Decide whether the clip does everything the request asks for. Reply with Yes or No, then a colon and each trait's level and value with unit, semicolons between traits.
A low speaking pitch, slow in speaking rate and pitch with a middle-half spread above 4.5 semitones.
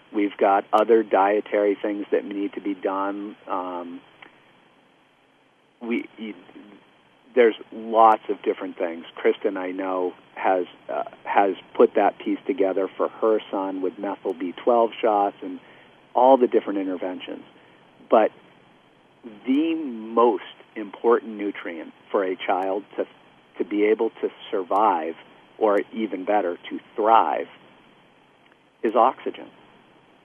No: low, 105 Hz; slow, 120 wpm; average, 2.8 semitones